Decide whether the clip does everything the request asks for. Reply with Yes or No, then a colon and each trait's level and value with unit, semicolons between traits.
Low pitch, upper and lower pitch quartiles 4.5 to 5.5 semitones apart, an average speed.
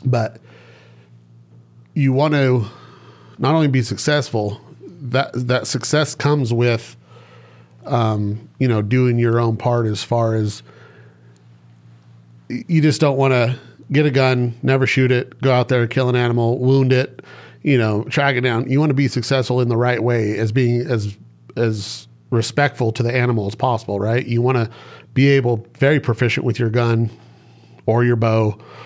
No: low, 120 Hz; average, 3.2 semitones; average, 165 wpm